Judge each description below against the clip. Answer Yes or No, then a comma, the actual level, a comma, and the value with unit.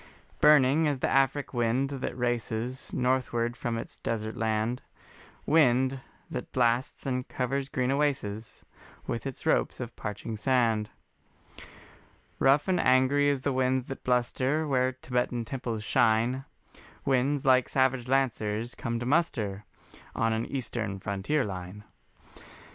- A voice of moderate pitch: No, low, 125 Hz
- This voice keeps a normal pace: No, slow, 130 wpm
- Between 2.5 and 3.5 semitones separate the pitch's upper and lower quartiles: Yes, average, 2.8 semitones